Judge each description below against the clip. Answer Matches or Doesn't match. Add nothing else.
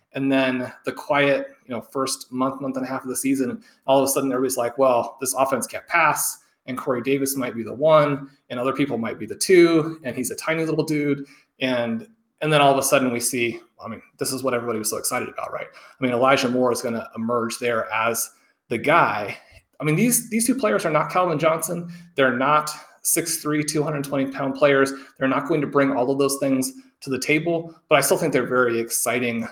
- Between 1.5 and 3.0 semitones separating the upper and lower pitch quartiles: Doesn't match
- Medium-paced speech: Doesn't match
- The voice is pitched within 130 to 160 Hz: Matches